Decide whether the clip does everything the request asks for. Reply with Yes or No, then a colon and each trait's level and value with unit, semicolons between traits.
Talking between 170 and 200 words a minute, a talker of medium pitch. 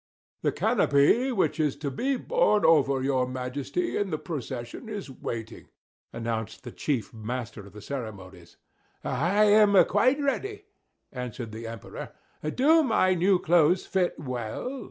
No: average, 140 wpm; medium, 145 Hz